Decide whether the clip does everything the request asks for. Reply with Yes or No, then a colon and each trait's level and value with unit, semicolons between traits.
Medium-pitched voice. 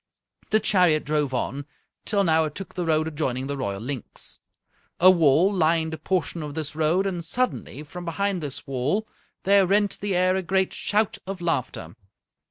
Yes: medium, 165 Hz